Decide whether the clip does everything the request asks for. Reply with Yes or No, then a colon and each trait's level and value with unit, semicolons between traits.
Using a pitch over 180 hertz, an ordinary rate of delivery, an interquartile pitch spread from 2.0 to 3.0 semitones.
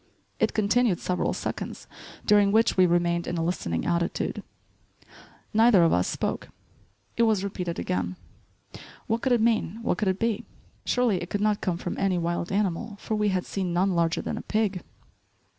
No: high, 190 Hz; average, 175 wpm; average, 3.7 semitones